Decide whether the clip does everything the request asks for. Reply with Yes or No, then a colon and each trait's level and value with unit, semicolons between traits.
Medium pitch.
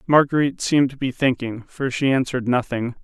No: low, 130 Hz